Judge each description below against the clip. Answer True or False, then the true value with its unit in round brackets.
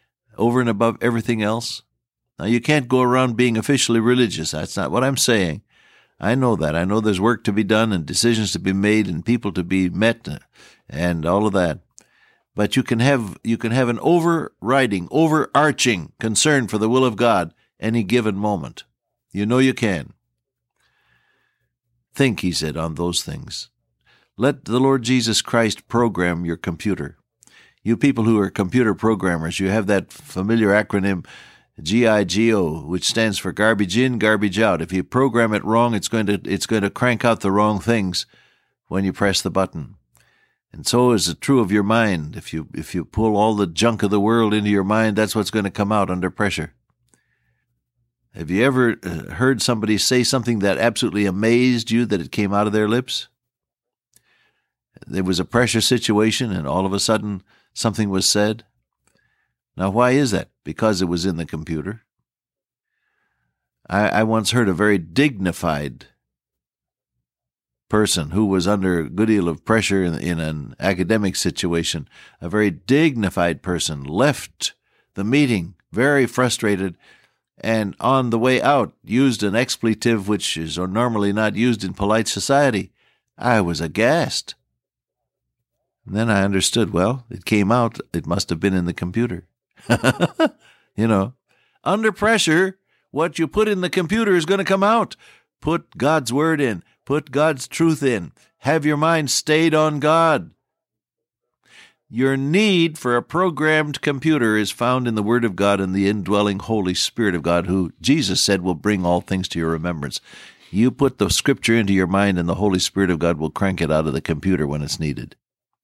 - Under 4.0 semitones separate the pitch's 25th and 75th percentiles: False (4.5 semitones)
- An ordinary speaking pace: True (175 wpm)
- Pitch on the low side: True (110 Hz)